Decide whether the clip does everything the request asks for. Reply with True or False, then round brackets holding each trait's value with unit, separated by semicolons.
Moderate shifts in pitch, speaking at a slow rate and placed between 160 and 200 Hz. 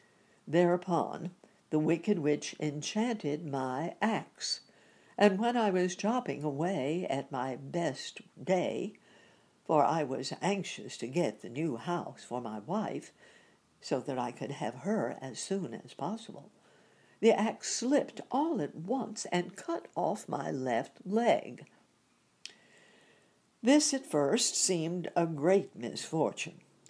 False (5.7 semitones; 130 wpm; 185 Hz)